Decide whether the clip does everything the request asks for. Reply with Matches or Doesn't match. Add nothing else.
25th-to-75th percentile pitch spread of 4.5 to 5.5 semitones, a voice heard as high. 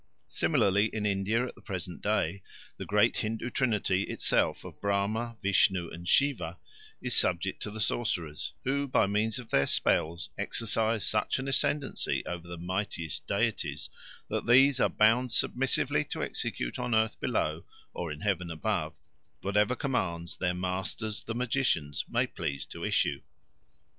Doesn't match